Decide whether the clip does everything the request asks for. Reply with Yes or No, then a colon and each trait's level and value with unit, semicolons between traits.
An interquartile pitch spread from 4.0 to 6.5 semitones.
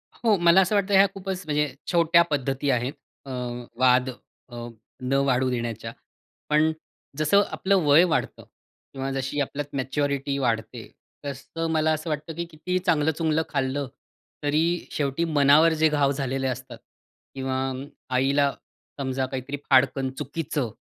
No: average, 3.3 semitones